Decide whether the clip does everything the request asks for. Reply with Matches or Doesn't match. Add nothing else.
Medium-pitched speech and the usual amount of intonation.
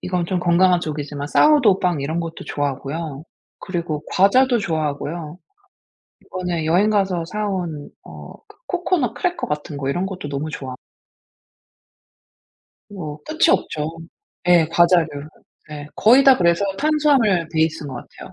Matches